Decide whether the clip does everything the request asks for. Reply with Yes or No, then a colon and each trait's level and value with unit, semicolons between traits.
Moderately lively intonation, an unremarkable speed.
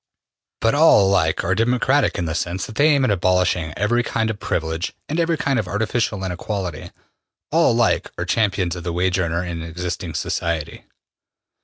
Yes: average, 4.8 semitones; average, 175 wpm